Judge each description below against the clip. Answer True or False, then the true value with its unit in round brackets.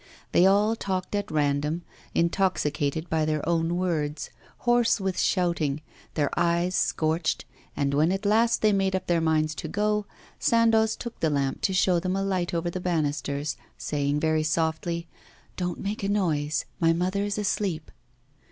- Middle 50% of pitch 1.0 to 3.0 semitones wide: False (3.9 semitones)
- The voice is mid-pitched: True (170 Hz)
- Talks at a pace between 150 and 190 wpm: True (160 wpm)